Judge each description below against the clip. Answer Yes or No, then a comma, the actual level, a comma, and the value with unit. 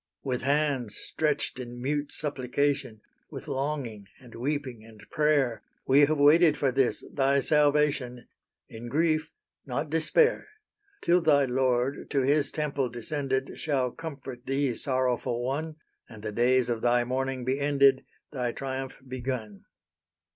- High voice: No, low, 135 Hz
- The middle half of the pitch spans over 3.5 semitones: No, average, 3.0 semitones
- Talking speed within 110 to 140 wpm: Yes, slow, 135 wpm